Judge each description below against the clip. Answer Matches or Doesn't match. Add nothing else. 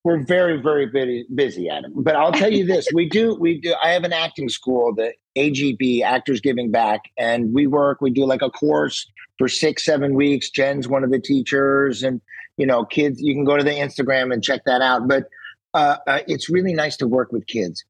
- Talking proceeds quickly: Matches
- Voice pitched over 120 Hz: Matches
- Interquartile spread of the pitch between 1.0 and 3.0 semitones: Matches